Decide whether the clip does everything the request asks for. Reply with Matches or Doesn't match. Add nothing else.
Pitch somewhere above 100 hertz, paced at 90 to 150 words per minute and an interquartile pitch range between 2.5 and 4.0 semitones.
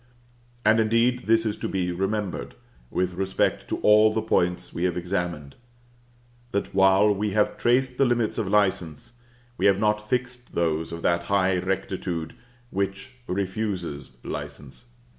Doesn't match